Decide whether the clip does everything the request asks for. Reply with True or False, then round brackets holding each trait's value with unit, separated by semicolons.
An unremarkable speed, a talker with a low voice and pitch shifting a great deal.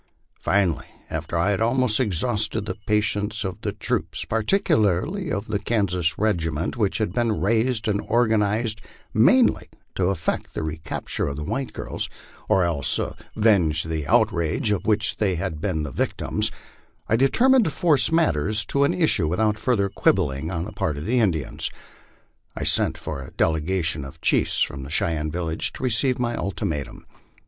True (160 wpm; 100 Hz; 5.7 semitones)